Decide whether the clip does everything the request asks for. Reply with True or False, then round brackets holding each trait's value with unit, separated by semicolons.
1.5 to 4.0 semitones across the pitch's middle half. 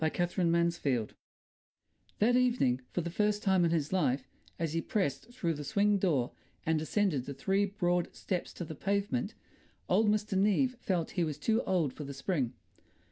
False (5.0 semitones)